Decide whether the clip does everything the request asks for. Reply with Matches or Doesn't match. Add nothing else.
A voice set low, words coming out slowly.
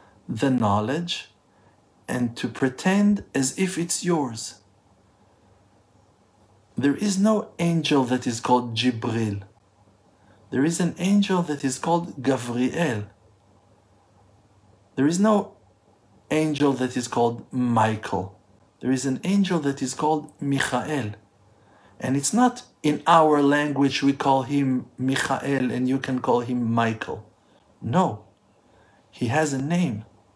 Matches